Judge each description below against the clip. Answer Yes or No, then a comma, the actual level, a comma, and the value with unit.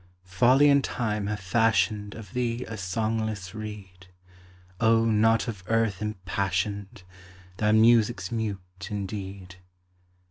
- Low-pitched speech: Yes, low, 105 Hz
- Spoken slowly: Yes, slow, 110 wpm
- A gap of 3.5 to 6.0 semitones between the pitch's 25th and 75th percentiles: No, average, 2.9 semitones